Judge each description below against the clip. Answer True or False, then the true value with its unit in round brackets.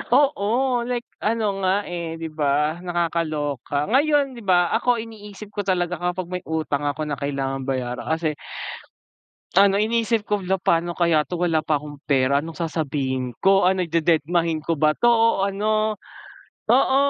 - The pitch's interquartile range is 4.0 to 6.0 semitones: True (5.2 semitones)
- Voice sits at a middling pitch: True (175 Hz)